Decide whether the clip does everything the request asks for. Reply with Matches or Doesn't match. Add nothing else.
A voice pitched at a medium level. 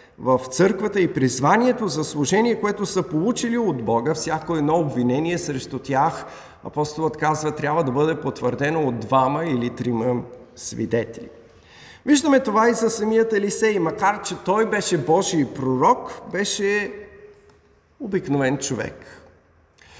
Matches